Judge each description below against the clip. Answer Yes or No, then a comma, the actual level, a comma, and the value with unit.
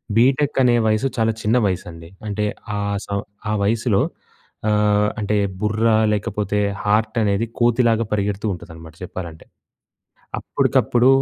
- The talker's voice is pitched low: Yes, low, 105 Hz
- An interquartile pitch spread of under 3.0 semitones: Yes, narrow, 2.5 semitones